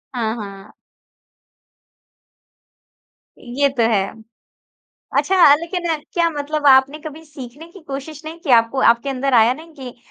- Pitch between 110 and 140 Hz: No, very high, 275 Hz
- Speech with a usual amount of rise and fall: Yes, average, 4.5 semitones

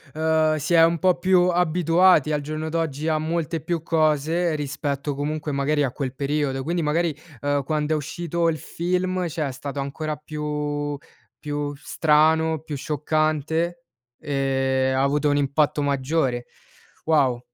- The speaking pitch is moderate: Yes, medium, 150 Hz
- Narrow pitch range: Yes, narrow, 2.3 semitones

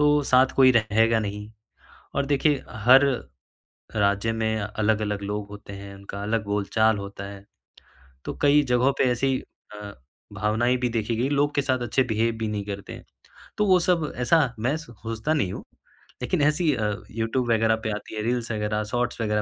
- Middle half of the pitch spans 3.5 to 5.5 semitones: Yes, average, 4.0 semitones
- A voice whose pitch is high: No, low, 115 Hz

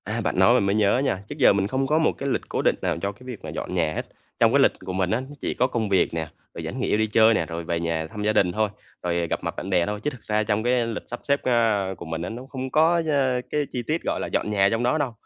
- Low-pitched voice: Yes, low, 110 Hz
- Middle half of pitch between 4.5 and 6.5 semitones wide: Yes, wide, 5.4 semitones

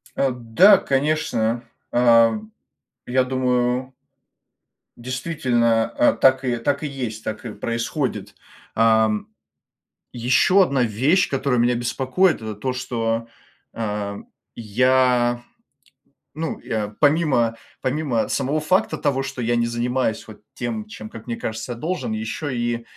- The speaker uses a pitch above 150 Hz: No, low, 125 Hz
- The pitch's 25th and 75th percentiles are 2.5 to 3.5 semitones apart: Yes, average, 2.9 semitones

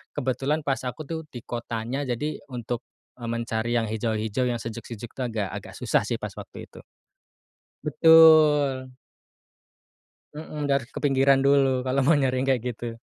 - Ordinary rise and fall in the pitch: Yes, average, 3.3 semitones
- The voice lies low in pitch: Yes, low, 130 Hz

